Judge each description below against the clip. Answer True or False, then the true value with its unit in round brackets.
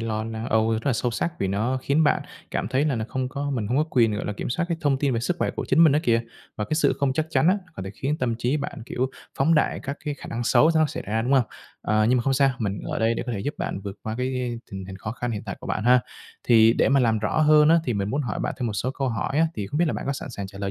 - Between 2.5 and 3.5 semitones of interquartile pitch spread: False (4.4 semitones)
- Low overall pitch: True (125 Hz)